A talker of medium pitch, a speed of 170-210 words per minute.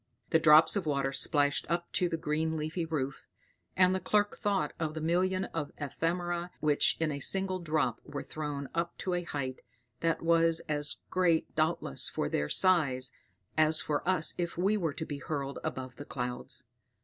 Yes: medium, 160 Hz; average, 180 wpm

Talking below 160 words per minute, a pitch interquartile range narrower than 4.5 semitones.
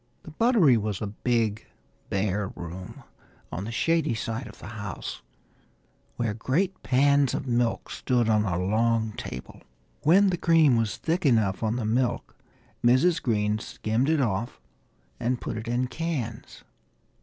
No: average, 150 wpm; average, 4.8 semitones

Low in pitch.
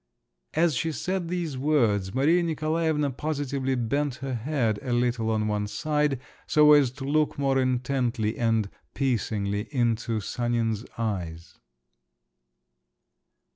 Yes: low, 130 Hz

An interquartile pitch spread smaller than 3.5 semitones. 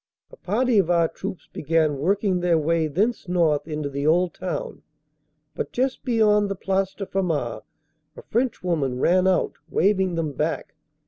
No: average, 3.9 semitones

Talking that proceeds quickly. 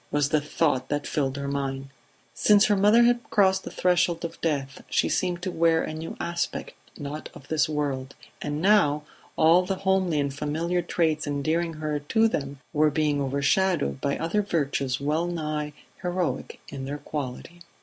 No: average, 170 wpm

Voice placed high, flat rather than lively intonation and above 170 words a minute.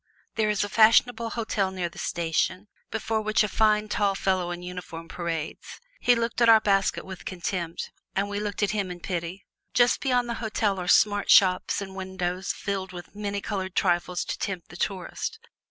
No: high, 195 Hz; average, 3.0 semitones; average, 185 wpm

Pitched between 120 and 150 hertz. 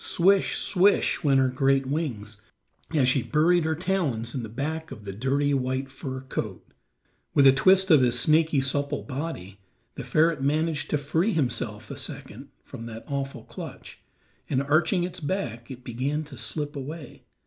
Yes: medium, 140 Hz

